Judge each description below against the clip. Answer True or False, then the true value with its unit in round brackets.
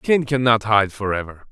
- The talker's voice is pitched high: False (115 Hz)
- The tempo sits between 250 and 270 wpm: False (200 wpm)